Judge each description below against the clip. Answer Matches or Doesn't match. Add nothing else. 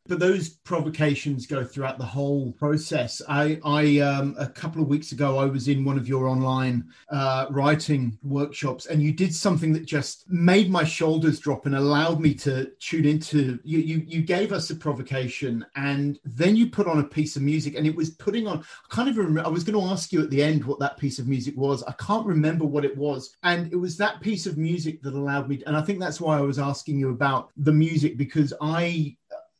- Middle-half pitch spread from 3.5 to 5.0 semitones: Doesn't match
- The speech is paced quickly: Matches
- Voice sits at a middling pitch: Matches